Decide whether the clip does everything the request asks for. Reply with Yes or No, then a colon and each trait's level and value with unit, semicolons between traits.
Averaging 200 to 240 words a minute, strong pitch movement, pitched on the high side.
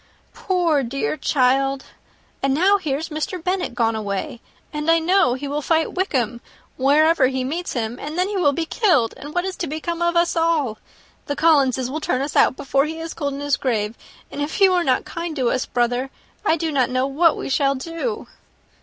No: fast, 205 wpm; average, 4.3 semitones; very high, 290 Hz